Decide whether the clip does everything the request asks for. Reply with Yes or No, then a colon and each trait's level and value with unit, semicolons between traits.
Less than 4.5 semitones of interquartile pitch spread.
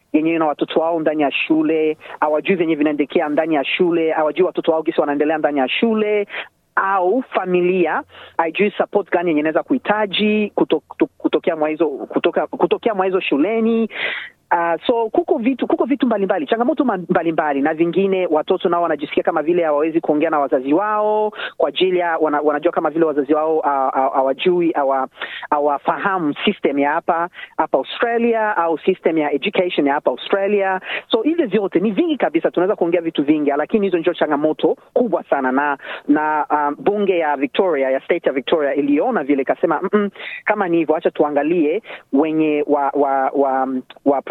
No: average, 5.2 semitones